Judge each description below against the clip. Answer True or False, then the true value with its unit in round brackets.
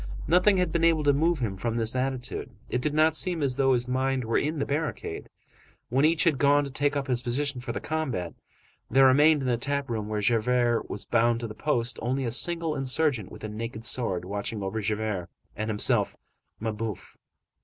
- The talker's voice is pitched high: False (125 Hz)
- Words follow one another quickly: True (210 wpm)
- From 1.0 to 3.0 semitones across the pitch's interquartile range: False (4.3 semitones)